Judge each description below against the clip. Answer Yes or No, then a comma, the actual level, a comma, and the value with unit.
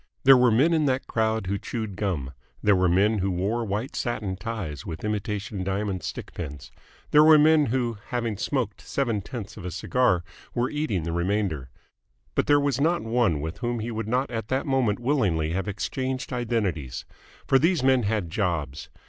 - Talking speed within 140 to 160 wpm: No, average, 185 wpm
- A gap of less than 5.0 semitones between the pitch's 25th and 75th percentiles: No, average, 5.3 semitones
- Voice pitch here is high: No, low, 110 Hz